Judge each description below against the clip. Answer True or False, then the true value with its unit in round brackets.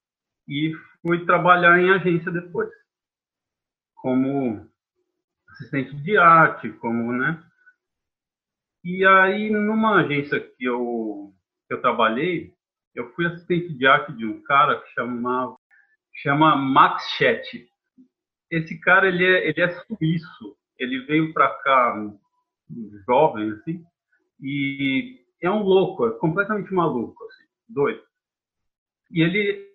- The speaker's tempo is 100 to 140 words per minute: True (120 wpm)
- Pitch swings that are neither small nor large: False (7.0 semitones)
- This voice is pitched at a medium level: True (170 Hz)